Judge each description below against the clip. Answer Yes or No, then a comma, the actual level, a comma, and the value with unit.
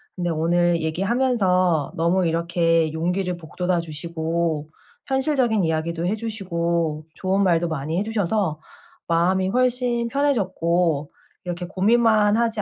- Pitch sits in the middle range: Yes, medium, 175 Hz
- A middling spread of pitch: Yes, average, 4.0 semitones